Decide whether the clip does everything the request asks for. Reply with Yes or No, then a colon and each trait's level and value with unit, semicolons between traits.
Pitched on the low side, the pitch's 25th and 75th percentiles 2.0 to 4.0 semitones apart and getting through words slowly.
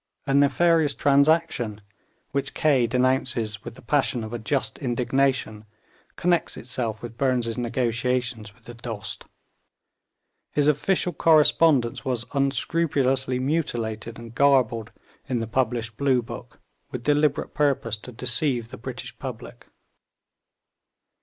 Yes: low, 125 Hz; average, 3.3 semitones; slow, 120 wpm